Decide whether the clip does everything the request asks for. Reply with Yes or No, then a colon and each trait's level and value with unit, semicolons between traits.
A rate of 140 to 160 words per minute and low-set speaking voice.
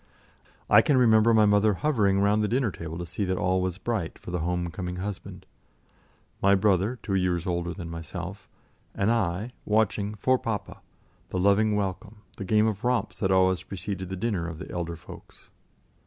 No: average, 185 wpm; low, 100 Hz